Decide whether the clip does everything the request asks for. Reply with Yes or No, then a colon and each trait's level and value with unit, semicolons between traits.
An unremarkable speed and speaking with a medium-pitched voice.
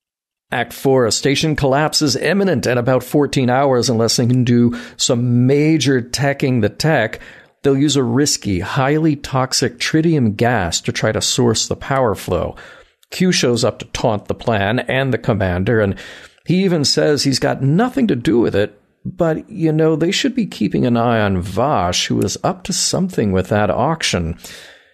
No: average, 180 wpm; low, 130 Hz